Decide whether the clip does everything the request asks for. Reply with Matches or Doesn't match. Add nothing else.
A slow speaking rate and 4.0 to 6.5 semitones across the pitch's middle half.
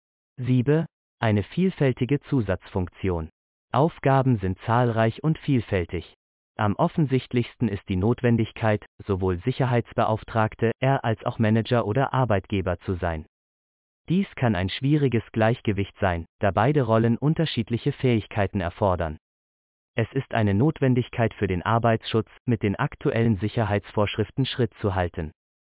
Matches